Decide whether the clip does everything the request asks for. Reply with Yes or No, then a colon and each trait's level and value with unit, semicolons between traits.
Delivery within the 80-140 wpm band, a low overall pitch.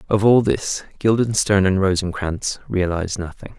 Yes: slow, 135 wpm; low, 100 Hz